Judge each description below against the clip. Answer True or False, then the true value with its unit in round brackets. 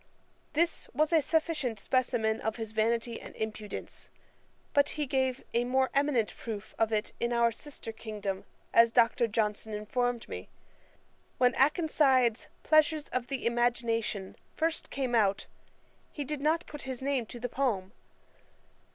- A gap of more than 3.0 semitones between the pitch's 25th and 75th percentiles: True (3.9 semitones)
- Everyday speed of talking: True (145 wpm)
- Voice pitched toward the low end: False (245 Hz)